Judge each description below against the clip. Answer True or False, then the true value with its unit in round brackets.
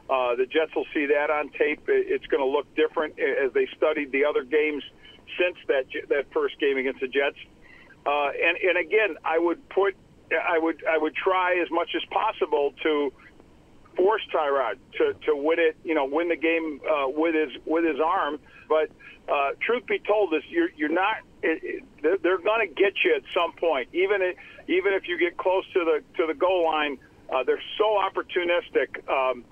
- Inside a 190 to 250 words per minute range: True (195 wpm)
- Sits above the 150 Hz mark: True (185 Hz)